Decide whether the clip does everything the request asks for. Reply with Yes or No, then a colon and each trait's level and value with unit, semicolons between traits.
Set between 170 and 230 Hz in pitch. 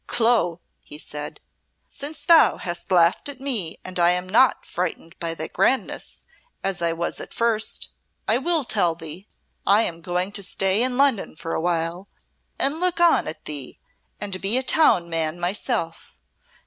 Yes: medium, 185 Hz